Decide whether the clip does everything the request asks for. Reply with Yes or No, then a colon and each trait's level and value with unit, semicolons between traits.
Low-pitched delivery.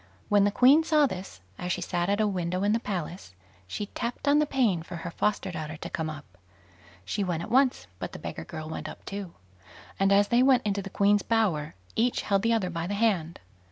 No: high, 195 Hz